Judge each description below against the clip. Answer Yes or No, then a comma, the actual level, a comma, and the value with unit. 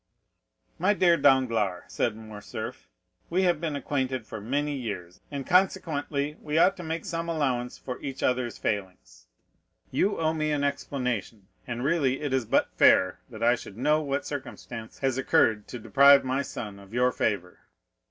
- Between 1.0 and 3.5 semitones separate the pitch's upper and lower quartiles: No, average, 4.8 semitones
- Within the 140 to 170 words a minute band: Yes, average, 165 wpm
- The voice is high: No, low, 135 Hz